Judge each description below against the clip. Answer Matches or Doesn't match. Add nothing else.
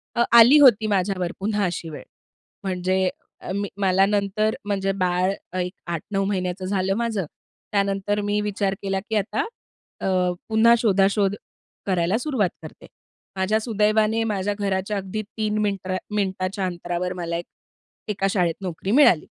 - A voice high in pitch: Matches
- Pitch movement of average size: Doesn't match